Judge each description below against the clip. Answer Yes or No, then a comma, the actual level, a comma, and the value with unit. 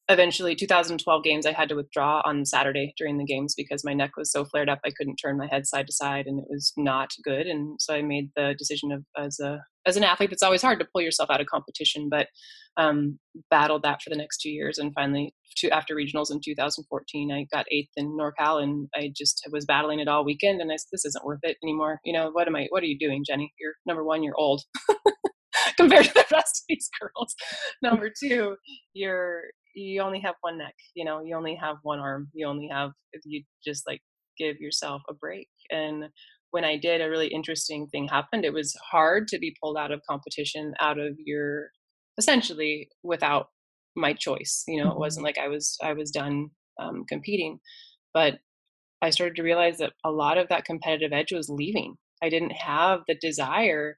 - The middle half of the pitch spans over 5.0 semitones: No, average, 2.9 semitones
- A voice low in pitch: No, medium, 150 Hz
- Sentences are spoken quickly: Yes, fast, 220 wpm